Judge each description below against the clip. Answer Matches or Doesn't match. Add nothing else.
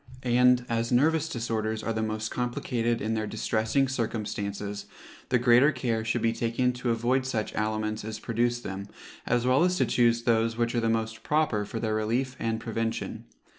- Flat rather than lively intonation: Matches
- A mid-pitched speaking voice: Doesn't match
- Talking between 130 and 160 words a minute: Doesn't match